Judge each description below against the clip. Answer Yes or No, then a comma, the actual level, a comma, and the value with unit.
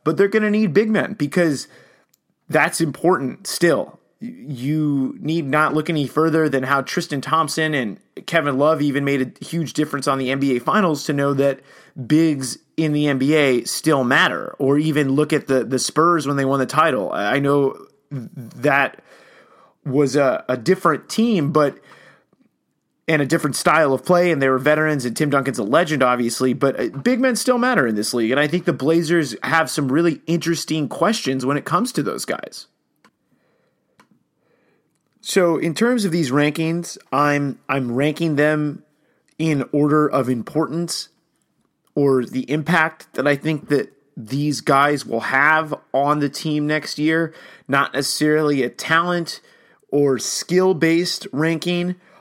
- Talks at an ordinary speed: Yes, average, 160 wpm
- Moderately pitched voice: Yes, medium, 150 Hz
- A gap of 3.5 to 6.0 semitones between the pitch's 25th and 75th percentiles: No, average, 3.1 semitones